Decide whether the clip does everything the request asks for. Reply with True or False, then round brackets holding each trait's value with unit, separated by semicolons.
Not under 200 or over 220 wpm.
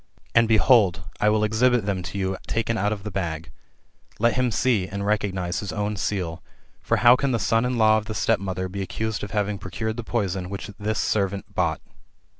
True (205 wpm)